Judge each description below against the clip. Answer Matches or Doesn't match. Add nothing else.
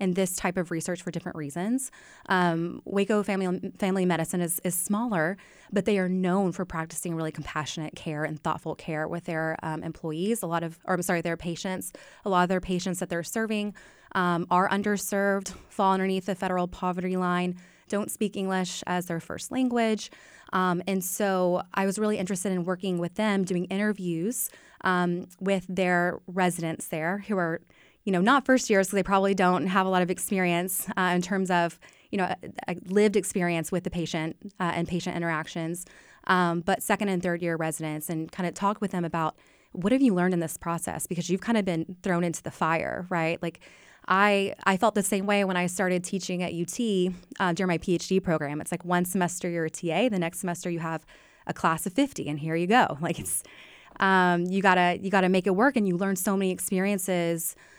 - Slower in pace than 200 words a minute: Doesn't match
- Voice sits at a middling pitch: Matches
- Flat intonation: Matches